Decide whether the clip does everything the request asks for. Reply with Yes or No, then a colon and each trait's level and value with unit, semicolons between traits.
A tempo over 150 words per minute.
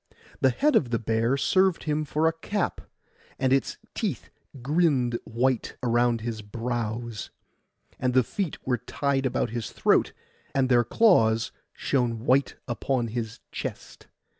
No: average, 140 wpm